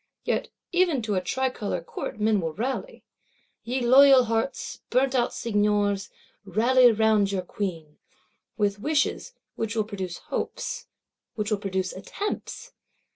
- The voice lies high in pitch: Yes, high, 220 Hz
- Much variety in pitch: No, average, 4.5 semitones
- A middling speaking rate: No, slow, 130 wpm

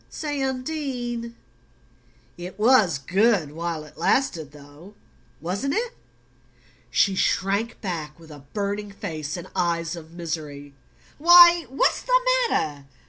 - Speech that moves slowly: Yes, slow, 120 wpm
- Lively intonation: Yes, wide, 7.5 semitones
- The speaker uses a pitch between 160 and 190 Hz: Yes, medium, 185 Hz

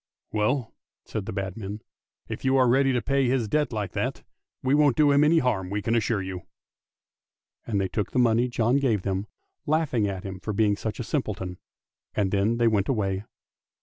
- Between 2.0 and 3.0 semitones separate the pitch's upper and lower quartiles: No, average, 4.7 semitones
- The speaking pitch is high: No, low, 110 Hz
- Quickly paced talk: Yes, fast, 210 wpm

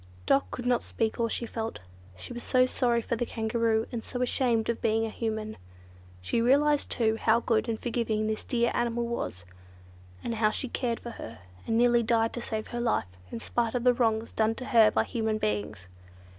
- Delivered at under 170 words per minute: No, fast, 205 wpm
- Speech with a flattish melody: Yes, narrow, 1.5 semitones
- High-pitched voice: Yes, high, 230 Hz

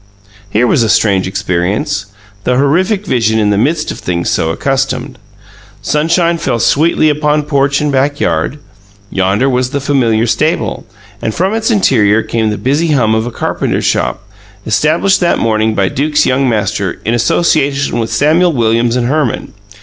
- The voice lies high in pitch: No, low, 125 Hz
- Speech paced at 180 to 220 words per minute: No, average, 160 wpm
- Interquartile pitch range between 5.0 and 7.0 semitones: Yes, average, 5.3 semitones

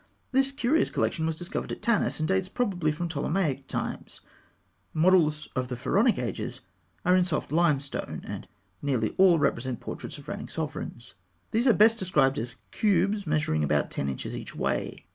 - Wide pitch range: Yes, wide, 6.3 semitones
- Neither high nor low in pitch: Yes, medium, 165 Hz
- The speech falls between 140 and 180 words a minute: Yes, average, 165 wpm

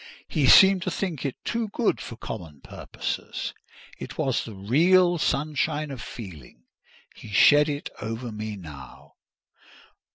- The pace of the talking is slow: Yes, slow, 130 wpm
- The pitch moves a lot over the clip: Yes, wide, 7.4 semitones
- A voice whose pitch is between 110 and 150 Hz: Yes, low, 135 Hz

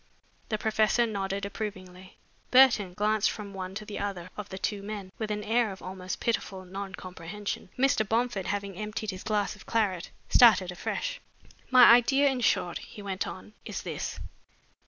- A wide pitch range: No, narrow, 2.5 semitones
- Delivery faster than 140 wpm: Yes, average, 170 wpm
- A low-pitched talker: No, high, 205 Hz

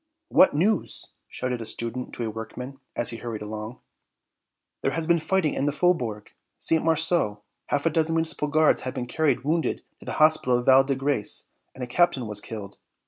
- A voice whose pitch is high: No, low, 135 Hz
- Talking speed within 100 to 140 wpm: No, average, 195 wpm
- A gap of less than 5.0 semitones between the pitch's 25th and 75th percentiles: No, average, 5.3 semitones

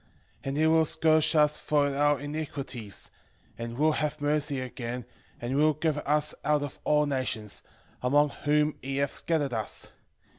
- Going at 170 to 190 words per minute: No, average, 160 wpm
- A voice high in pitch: No, medium, 145 Hz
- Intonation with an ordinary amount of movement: No, narrow, 2.2 semitones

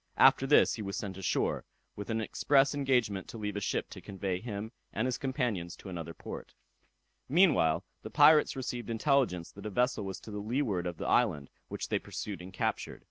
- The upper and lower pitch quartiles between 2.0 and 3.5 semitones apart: No, average, 5.1 semitones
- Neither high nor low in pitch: No, low, 105 Hz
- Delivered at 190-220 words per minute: Yes, average, 195 wpm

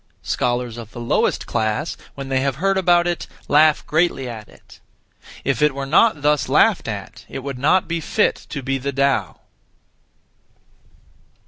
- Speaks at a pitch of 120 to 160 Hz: Yes, medium, 140 Hz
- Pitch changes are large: No, average, 4.0 semitones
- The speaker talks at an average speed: Yes, average, 160 wpm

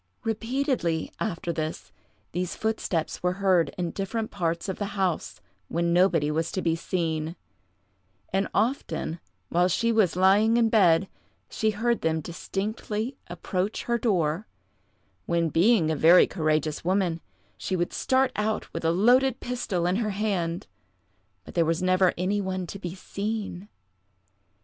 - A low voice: No, medium, 185 Hz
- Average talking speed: Yes, average, 145 wpm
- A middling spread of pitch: Yes, average, 4.2 semitones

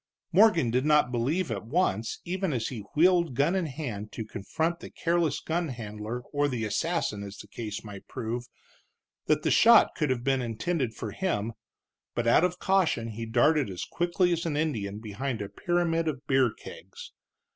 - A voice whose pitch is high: No, low, 130 Hz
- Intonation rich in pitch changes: Yes, wide, 7.0 semitones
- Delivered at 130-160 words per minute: No, average, 180 wpm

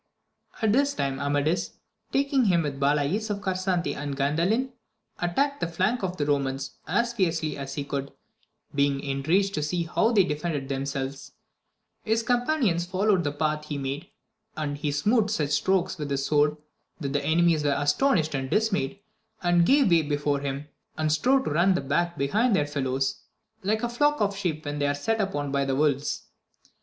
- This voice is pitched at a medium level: Yes, medium, 155 Hz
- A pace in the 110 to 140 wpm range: No, average, 180 wpm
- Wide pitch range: Yes, wide, 5.7 semitones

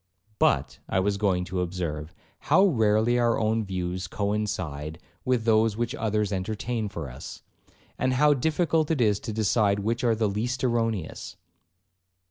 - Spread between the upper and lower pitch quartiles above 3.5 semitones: Yes, average, 4.1 semitones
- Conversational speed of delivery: Yes, average, 150 wpm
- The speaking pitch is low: Yes, low, 110 Hz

